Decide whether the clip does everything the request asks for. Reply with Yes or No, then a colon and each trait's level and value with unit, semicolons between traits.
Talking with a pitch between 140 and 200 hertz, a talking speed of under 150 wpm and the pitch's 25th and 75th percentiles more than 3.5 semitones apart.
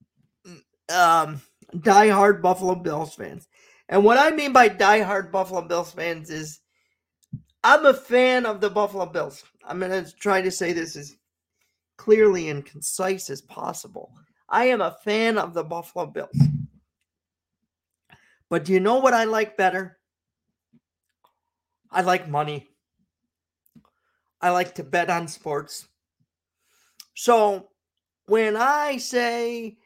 Yes: high, 190 Hz; slow, 135 wpm; average, 4.9 semitones